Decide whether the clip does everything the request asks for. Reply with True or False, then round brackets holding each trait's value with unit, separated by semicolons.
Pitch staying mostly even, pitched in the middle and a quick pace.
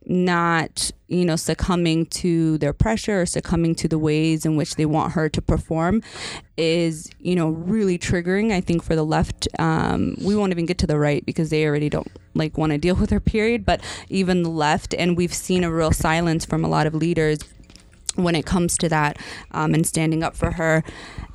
True (2.0 semitones; 165 Hz; 210 wpm)